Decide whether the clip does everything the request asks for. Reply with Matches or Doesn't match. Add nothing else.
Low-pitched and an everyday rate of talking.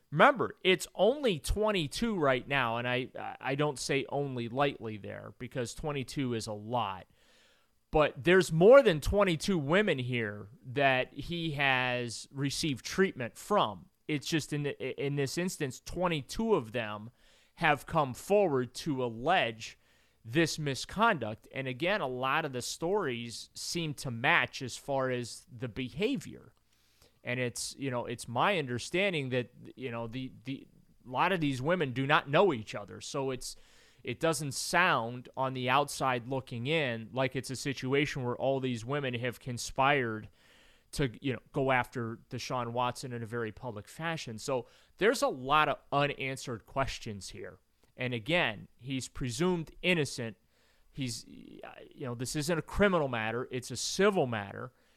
Matches